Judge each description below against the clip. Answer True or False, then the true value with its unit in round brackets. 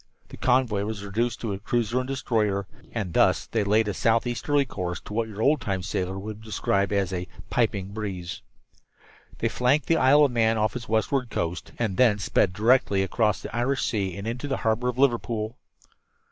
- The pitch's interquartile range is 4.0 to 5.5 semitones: False (3.6 semitones)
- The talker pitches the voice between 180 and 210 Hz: False (110 Hz)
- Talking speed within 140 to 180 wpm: False (195 wpm)